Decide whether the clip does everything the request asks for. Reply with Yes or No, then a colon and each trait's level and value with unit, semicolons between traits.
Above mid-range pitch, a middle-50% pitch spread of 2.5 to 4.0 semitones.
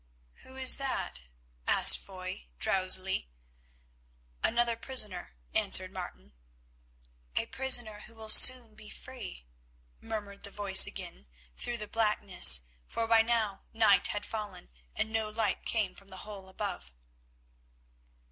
Yes: high, 210 Hz; average, 3.2 semitones